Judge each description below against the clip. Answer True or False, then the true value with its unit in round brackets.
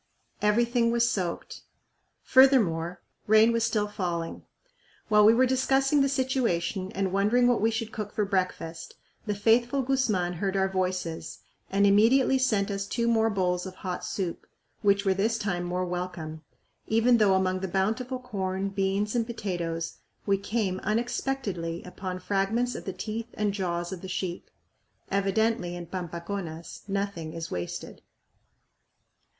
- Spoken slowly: False (145 wpm)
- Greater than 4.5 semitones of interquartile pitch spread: False (3.9 semitones)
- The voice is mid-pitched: False (200 Hz)